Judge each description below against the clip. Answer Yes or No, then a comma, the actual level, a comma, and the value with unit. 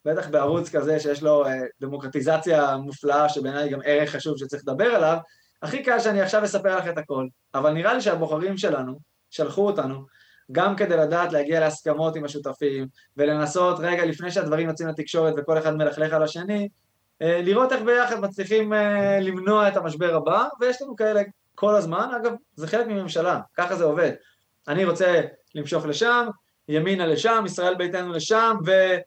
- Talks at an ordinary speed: No, fast, 160 wpm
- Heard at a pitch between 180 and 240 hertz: No, medium, 165 Hz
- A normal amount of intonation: Yes, average, 5.0 semitones